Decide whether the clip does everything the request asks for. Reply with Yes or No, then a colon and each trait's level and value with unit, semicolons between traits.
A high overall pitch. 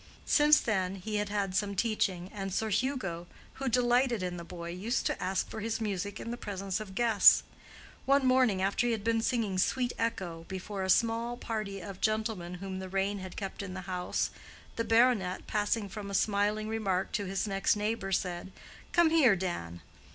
Yes: high, 205 Hz